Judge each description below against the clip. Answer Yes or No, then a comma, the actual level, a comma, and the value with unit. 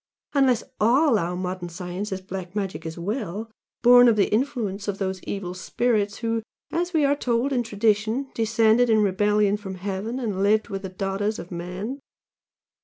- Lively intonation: No, average, 3.5 semitones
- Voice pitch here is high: Yes, high, 210 Hz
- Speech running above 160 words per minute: Yes, average, 175 wpm